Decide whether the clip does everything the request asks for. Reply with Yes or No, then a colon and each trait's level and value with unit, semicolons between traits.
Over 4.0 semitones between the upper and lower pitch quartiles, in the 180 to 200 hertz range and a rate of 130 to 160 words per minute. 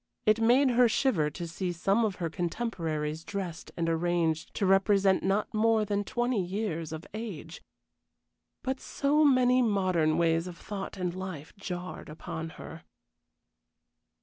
Yes: average, 4.8 semitones; high, 190 Hz; average, 145 wpm